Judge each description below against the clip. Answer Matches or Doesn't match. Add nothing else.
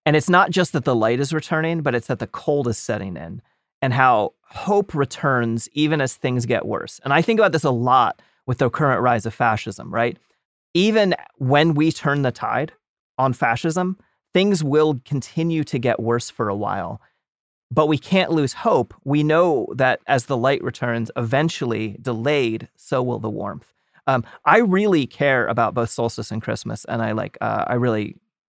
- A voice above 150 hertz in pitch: Doesn't match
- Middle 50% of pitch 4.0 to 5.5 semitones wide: Matches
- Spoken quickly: Doesn't match